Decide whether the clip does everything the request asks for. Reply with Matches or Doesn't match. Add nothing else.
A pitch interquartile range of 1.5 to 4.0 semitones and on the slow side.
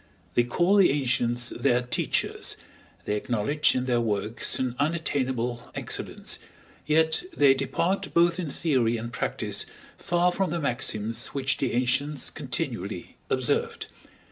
Doesn't match